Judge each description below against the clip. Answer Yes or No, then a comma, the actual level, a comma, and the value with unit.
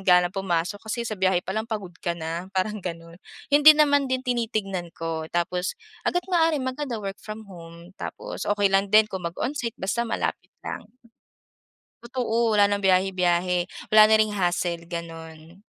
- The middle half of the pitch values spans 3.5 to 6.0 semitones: Yes, average, 4.2 semitones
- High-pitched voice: Yes, high, 195 Hz